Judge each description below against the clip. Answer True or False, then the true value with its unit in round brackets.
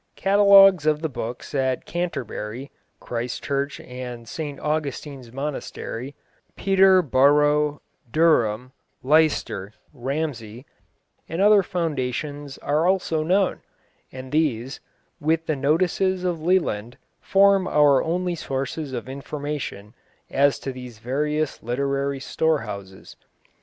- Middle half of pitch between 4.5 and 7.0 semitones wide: False (4.1 semitones)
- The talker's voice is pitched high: False (145 Hz)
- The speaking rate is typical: False (105 wpm)